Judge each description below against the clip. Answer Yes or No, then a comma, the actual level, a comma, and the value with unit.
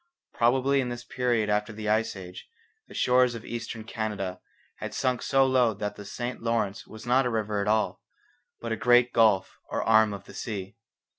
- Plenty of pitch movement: No, average, 2.7 semitones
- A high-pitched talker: No, low, 115 Hz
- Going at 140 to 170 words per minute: No, average, 195 wpm